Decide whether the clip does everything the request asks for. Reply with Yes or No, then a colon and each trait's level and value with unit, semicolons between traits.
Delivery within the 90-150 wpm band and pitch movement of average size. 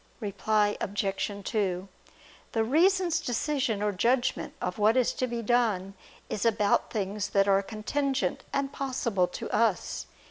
Yes: average, 140 wpm; average, 4.1 semitones